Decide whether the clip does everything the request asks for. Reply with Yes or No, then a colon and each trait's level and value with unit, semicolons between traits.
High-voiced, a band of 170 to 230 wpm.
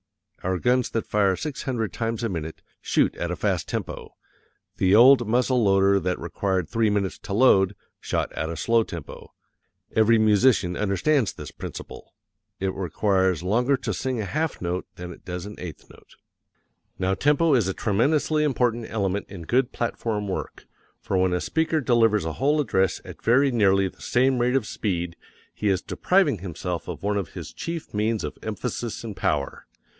No: low, 105 Hz; average, 180 wpm